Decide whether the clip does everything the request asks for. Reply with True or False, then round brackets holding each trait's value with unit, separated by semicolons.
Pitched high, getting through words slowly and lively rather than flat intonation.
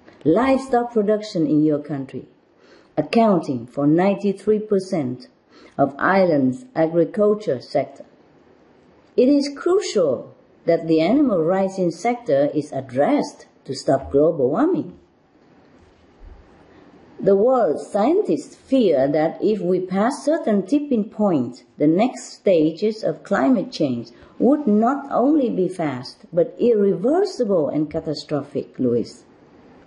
True (195 Hz; 105 wpm; 7.9 semitones)